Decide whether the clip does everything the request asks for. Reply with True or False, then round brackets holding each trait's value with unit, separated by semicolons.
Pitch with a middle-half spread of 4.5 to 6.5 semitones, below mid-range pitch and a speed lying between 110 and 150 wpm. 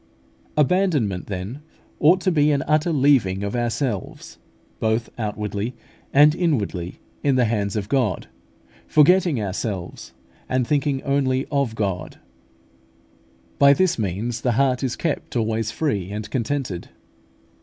True (5.5 semitones; 125 Hz; 135 wpm)